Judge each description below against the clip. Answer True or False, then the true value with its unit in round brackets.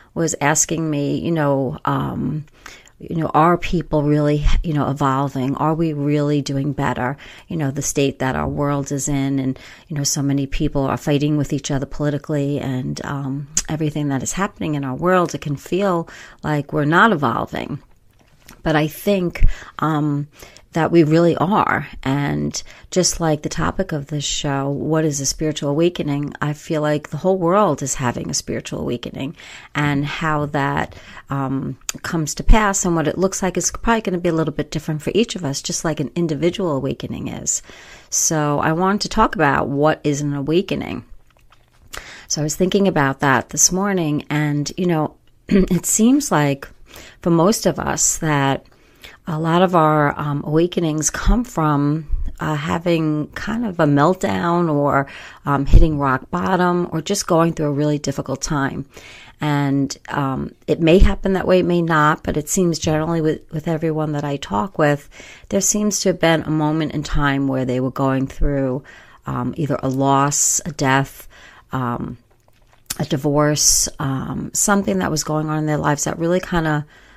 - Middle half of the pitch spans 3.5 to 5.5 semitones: False (3.1 semitones)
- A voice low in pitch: False (150 Hz)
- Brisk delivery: False (180 wpm)